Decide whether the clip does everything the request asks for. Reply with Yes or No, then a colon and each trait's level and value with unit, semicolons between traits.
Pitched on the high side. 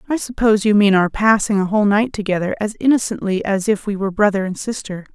Yes: high, 205 Hz